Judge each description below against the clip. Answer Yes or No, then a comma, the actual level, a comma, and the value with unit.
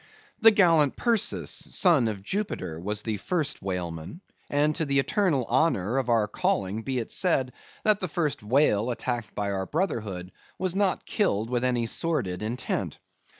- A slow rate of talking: No, average, 165 wpm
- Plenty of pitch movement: Yes, wide, 8.0 semitones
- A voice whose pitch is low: Yes, low, 125 Hz